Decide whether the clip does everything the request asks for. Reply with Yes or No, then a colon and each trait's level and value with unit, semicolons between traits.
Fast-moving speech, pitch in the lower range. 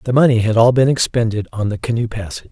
Yes: fast, 240 wpm; low, 115 Hz